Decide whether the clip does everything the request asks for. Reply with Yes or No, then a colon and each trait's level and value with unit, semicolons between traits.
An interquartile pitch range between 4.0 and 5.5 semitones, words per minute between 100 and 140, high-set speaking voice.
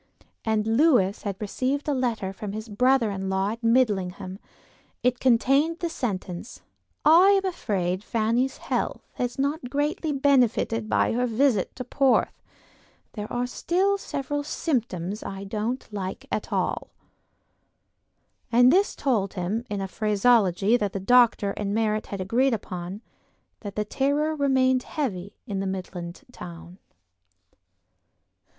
Yes: average, 5.1 semitones; slow, 135 wpm; high, 230 Hz